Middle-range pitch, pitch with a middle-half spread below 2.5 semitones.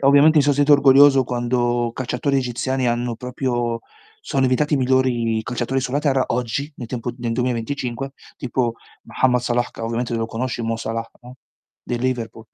No: low, 125 Hz; narrow, 2.1 semitones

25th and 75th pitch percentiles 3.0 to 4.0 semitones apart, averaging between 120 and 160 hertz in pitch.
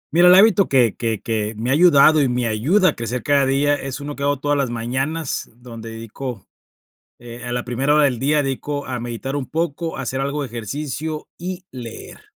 Yes: average, 3.6 semitones; low, 135 Hz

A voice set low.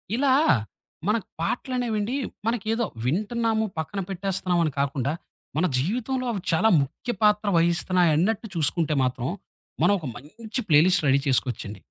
No: medium, 185 Hz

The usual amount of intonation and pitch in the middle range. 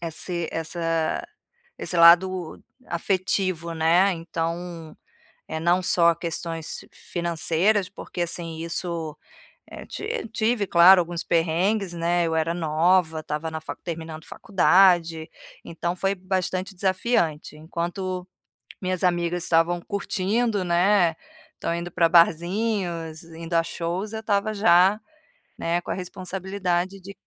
No: narrow, 2.1 semitones; medium, 175 Hz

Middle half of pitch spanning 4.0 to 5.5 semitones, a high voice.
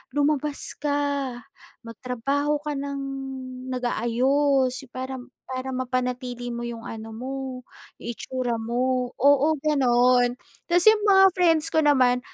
No: narrow, 2.6 semitones; very high, 260 Hz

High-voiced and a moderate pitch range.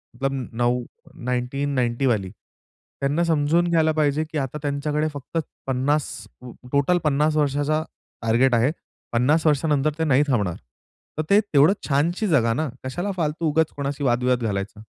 No: medium, 140 Hz; average, 3.4 semitones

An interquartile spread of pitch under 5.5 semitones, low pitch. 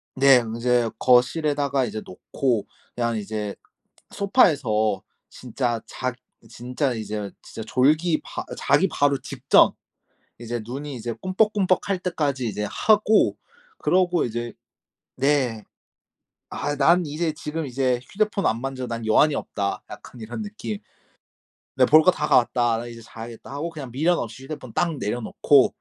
Yes: average, 5.1 semitones; low, 130 Hz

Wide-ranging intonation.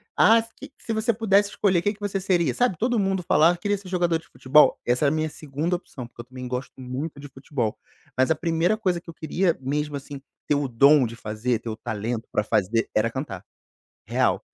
Yes: wide, 6.8 semitones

